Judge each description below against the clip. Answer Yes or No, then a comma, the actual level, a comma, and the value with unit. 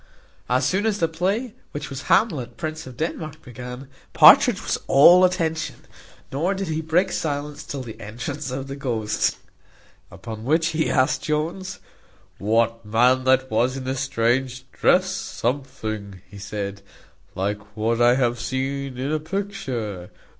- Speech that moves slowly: No, average, 150 wpm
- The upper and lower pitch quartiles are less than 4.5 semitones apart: No, average, 5.2 semitones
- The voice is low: Yes, low, 130 Hz